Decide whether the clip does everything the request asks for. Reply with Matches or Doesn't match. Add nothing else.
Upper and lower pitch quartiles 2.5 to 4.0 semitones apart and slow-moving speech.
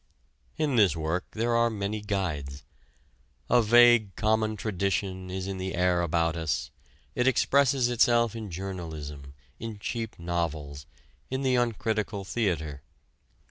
Doesn't match